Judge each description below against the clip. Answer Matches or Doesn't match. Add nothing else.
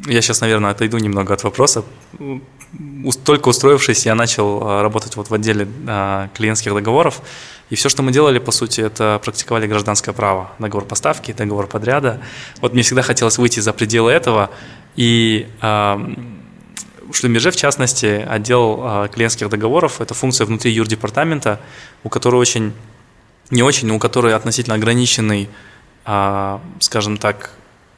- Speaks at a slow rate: Doesn't match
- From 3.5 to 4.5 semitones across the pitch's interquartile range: Doesn't match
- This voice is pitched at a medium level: Doesn't match